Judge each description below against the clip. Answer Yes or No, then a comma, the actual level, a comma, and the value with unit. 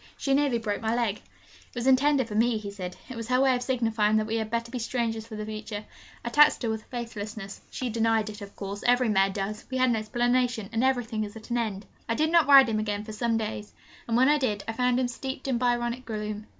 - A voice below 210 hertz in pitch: No, high, 230 Hz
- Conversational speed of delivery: No, fast, 255 wpm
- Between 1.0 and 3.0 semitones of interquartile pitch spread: Yes, average, 2.7 semitones